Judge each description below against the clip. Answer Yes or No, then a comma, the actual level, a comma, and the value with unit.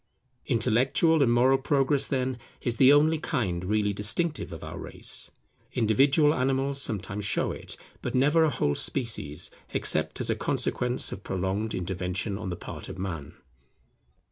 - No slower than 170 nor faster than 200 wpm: No, average, 150 wpm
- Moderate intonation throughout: No, wide, 5.9 semitones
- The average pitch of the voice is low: Yes, low, 120 Hz